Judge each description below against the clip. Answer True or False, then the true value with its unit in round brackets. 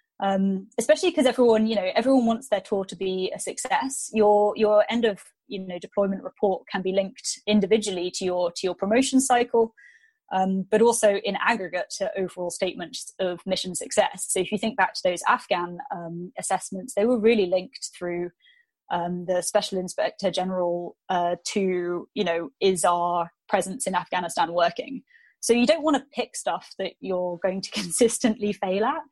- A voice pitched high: True (200 Hz)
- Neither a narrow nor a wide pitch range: True (3.9 semitones)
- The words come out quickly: False (180 wpm)